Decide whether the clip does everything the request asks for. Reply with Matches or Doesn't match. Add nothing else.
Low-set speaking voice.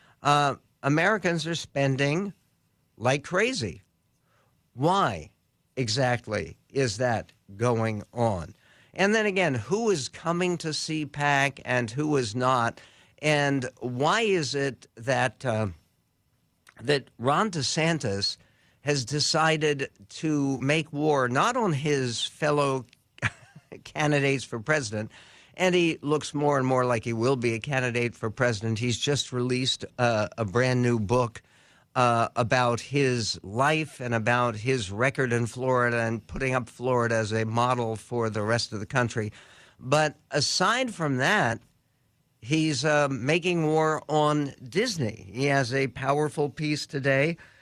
Matches